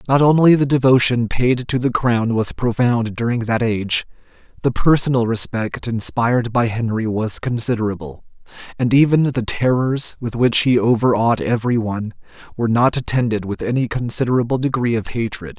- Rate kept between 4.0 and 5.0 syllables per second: No, 5.4 syllables/s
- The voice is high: No, low, 120 Hz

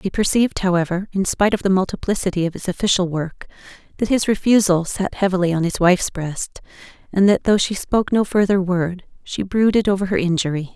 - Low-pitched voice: No, high, 190 Hz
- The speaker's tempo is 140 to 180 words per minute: No, average, 190 wpm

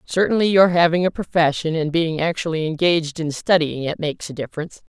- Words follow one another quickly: No, average, 180 wpm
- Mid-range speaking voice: Yes, medium, 165 Hz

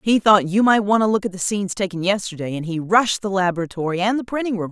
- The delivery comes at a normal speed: No, fast, 265 wpm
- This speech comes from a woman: Yes, female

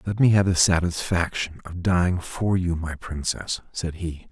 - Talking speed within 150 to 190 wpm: Yes, average, 180 wpm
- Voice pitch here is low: Yes, very low, 85 Hz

